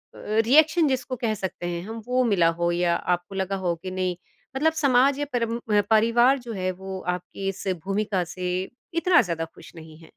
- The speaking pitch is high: Yes, high, 205 Hz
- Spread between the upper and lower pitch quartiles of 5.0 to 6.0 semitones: Yes, wide, 5.5 semitones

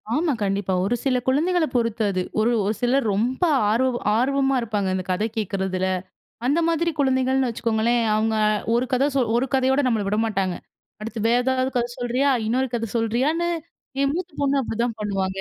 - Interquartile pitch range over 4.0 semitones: No, average, 3.7 semitones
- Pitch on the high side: Yes, high, 240 Hz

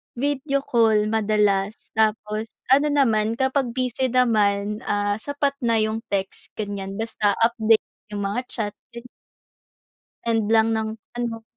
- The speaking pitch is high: Yes, high, 220 Hz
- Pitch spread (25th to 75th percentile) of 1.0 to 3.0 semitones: Yes, narrow, 2.5 semitones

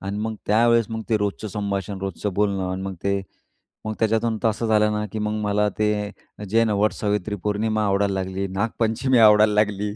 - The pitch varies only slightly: Yes, narrow, 1.7 semitones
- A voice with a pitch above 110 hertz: No, low, 105 Hz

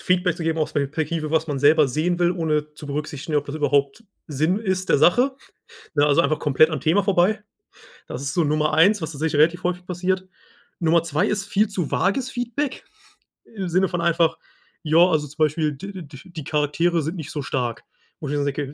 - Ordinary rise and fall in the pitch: Yes, average, 3.4 semitones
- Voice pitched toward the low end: No, medium, 160 Hz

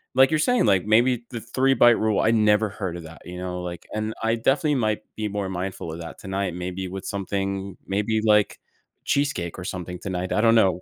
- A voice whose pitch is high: No, low, 100 Hz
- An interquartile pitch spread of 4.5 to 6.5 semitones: No, average, 3.5 semitones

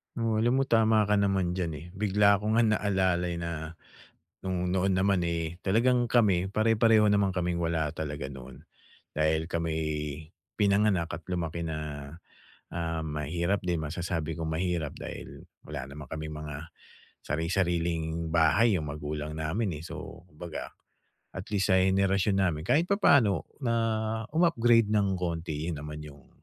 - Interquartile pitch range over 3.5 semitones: Yes, average, 4.2 semitones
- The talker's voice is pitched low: Yes, very low, 85 Hz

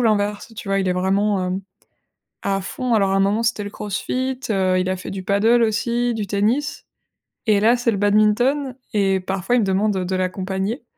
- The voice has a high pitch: Yes, high, 205 Hz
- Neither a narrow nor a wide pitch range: Yes, average, 3.1 semitones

